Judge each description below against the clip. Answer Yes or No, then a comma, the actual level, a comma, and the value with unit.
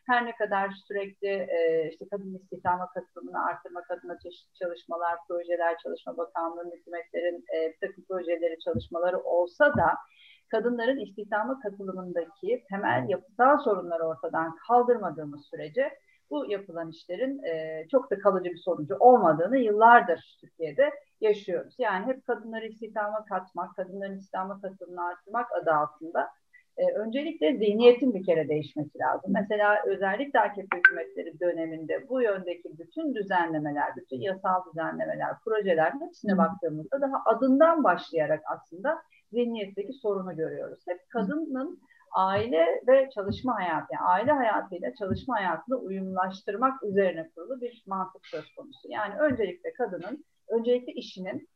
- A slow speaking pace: No, average, 125 wpm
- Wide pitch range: Yes, wide, 6.0 semitones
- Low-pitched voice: No, high, 195 Hz